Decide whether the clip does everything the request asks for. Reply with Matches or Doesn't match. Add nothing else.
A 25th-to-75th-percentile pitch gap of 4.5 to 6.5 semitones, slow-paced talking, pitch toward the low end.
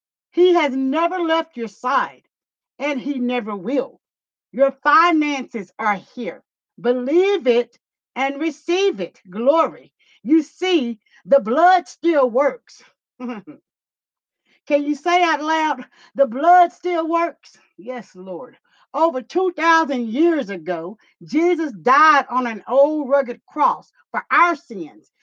Doesn't match